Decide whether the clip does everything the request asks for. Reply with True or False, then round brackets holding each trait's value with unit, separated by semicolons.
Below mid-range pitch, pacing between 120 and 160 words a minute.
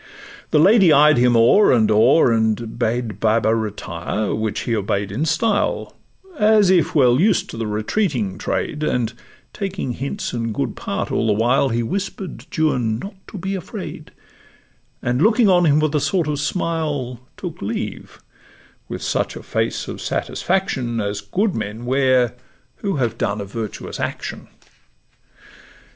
True (125 Hz; 155 wpm)